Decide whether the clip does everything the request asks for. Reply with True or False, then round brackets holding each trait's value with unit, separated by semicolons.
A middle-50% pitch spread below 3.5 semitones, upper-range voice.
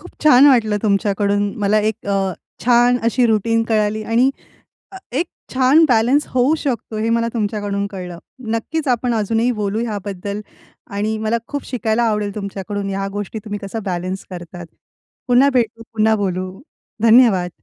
True (2.9 semitones; 215 Hz)